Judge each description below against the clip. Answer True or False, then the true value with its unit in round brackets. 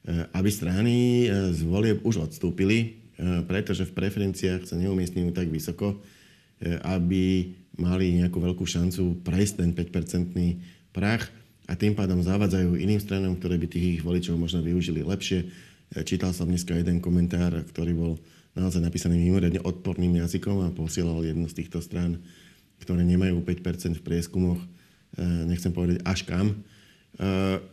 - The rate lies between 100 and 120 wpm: False (135 wpm)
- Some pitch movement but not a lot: False (1.6 semitones)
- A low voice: True (90 Hz)